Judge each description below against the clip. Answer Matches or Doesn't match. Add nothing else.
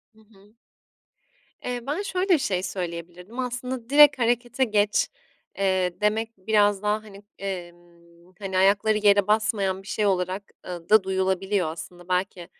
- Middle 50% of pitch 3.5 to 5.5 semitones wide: Doesn't match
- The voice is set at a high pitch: Matches